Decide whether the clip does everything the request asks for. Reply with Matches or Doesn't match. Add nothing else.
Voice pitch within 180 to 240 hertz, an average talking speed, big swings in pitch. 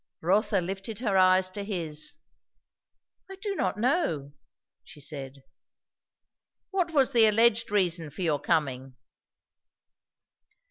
Doesn't match